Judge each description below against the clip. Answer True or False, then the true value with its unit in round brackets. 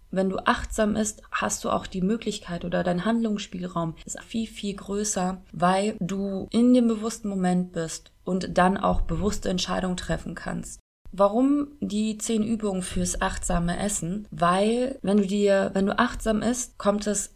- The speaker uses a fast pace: False (160 wpm)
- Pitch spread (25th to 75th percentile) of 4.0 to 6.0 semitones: False (3.0 semitones)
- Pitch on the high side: True (200 Hz)